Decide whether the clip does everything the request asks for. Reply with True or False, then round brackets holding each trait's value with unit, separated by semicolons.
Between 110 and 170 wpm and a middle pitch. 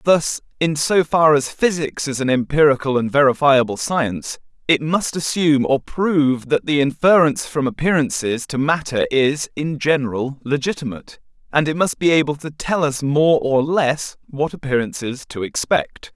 True (160 wpm; 145 Hz)